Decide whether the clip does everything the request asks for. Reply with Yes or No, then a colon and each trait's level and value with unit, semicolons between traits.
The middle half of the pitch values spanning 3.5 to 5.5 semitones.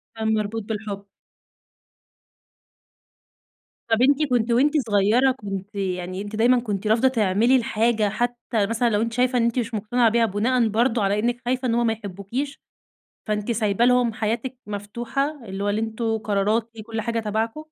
No: narrow, 2.6 semitones